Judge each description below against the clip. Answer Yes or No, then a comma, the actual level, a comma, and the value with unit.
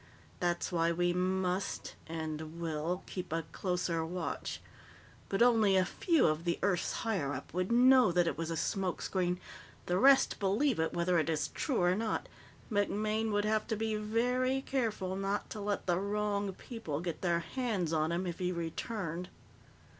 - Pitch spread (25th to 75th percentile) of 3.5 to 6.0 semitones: Yes, average, 4.0 semitones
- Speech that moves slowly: No, average, 175 wpm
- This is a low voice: No, medium, 185 Hz